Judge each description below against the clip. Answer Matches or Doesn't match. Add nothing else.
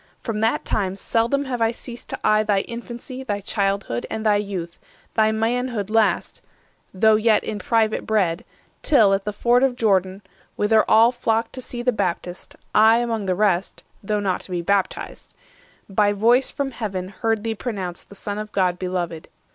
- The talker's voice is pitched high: Matches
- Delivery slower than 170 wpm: Doesn't match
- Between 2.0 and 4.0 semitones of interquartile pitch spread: Matches